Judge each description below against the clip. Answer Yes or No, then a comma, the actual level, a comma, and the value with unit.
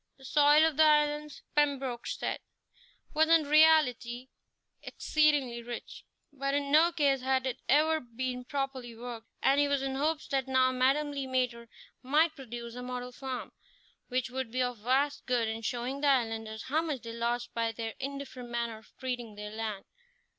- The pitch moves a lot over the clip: No, average, 3.2 semitones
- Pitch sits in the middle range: No, very high, 260 Hz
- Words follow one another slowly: No, average, 175 wpm